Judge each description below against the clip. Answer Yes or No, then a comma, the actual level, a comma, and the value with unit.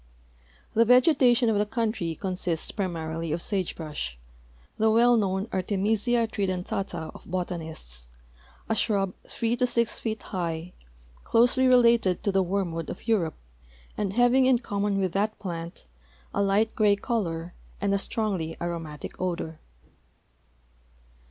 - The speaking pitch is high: Yes, high, 195 Hz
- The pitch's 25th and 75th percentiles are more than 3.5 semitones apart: Yes, average, 4.7 semitones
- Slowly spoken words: Yes, slow, 130 wpm